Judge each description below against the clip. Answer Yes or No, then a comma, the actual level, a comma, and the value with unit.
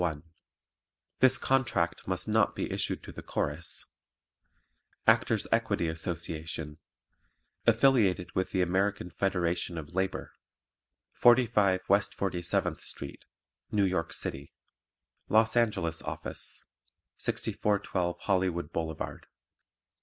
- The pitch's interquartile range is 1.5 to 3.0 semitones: No, average, 3.6 semitones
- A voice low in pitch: Yes, very low, 95 Hz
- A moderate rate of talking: No, slow, 100 wpm